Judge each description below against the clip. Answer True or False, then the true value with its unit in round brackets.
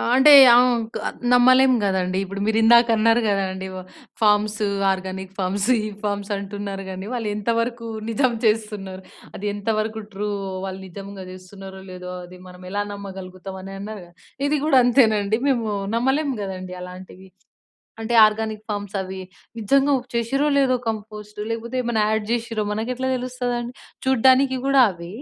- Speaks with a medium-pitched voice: False (210 Hz)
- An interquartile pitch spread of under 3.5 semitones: False (3.8 semitones)